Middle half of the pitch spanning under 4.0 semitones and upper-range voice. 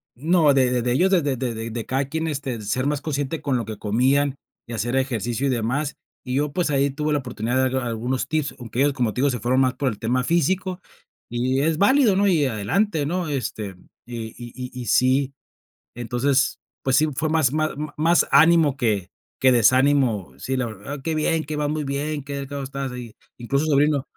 No: average, 3.5 semitones; low, 135 Hz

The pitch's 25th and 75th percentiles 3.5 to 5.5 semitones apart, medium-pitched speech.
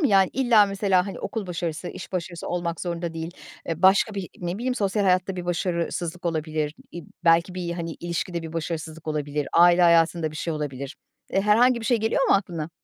No: average, 2.8 semitones; medium, 175 Hz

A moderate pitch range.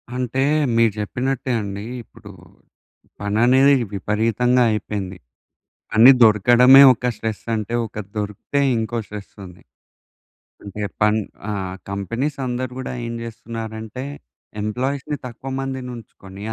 Yes: average, 3.3 semitones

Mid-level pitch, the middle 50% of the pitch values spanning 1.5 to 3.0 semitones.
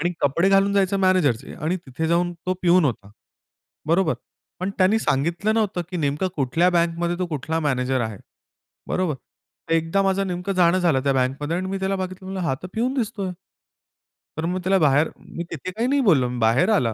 No: medium, 175 Hz; average, 4.5 semitones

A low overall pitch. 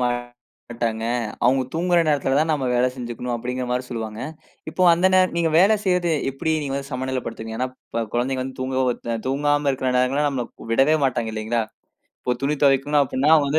Yes: low, 130 Hz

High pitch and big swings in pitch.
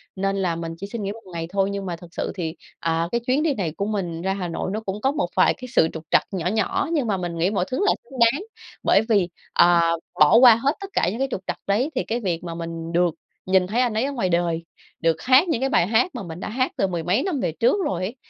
Yes: high, 195 Hz; wide, 5.7 semitones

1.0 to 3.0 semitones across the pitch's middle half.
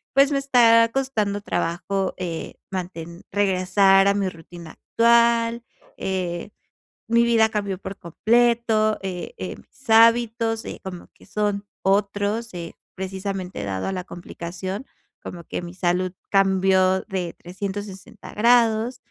No: average, 3.7 semitones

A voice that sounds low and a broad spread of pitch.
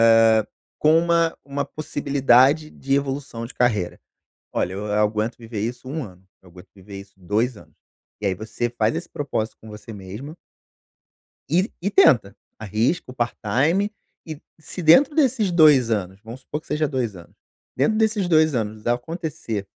Yes: low, 125 Hz; wide, 6.5 semitones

